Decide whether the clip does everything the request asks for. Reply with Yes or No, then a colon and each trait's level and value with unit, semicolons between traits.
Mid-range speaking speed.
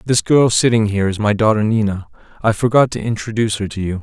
No: fast, 225 wpm